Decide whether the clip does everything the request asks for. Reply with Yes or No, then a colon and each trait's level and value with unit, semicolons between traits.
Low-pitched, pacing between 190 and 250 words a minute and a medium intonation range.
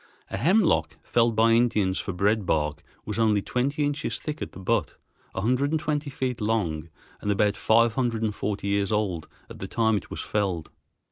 Yes: low, 110 Hz; average, 195 wpm; average, 4.0 semitones